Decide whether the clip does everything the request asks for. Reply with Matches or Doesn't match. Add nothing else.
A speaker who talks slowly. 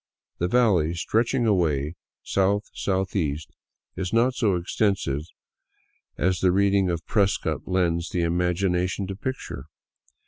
Matches